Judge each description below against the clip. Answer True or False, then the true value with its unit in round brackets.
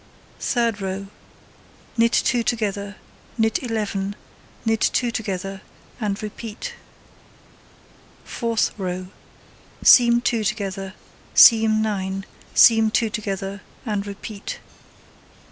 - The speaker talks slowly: True (95 wpm)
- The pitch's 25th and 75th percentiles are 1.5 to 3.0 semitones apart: True (2.5 semitones)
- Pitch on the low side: False (210 Hz)